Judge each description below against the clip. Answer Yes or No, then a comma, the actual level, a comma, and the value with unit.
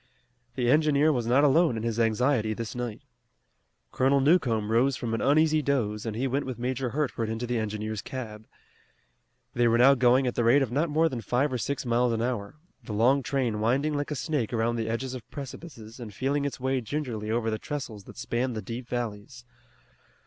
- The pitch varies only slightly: No, average, 3.4 semitones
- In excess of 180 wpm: Yes, fast, 205 wpm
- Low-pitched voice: Yes, low, 125 Hz